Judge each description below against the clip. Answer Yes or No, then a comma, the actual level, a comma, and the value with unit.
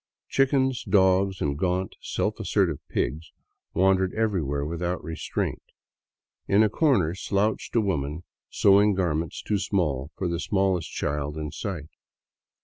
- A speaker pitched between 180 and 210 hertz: No, very low, 95 Hz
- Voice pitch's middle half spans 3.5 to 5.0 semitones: Yes, average, 4.1 semitones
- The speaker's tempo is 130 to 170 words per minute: Yes, average, 140 wpm